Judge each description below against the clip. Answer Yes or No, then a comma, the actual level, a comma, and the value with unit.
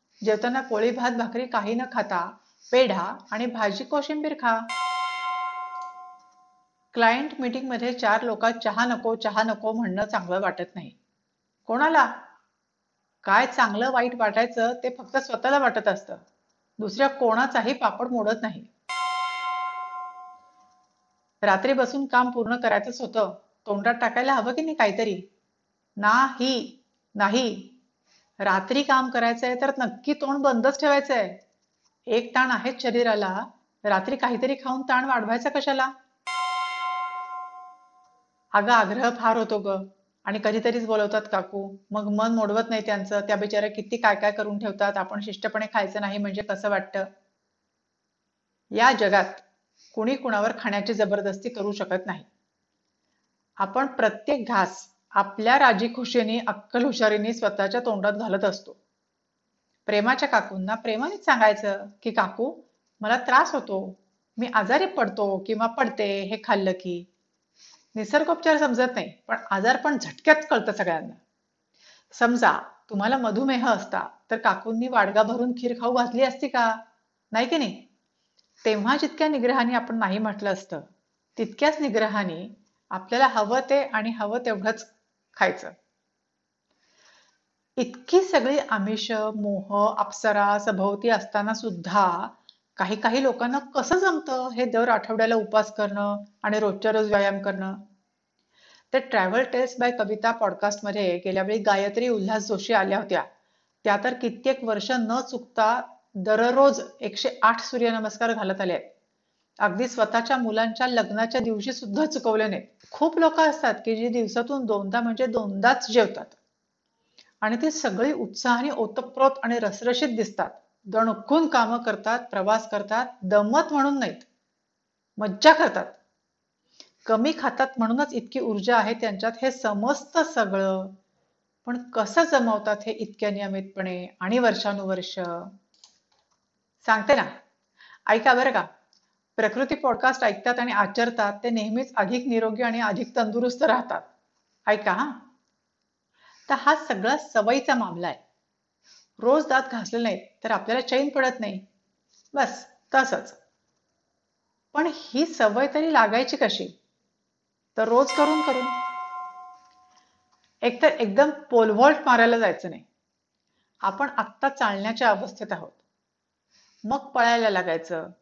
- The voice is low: No, high, 230 Hz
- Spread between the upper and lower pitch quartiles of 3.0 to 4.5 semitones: Yes, average, 3.8 semitones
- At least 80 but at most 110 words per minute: No, average, 120 wpm